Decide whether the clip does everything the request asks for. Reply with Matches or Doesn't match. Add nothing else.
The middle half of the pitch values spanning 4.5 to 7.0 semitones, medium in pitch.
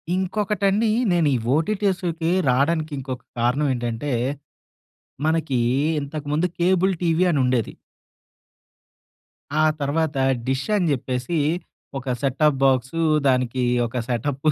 Matches